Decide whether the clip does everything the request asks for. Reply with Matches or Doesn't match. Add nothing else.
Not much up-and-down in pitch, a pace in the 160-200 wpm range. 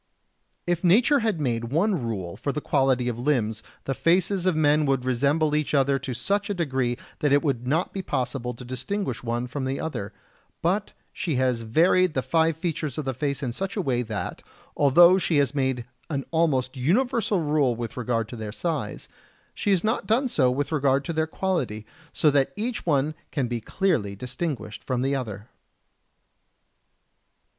Doesn't match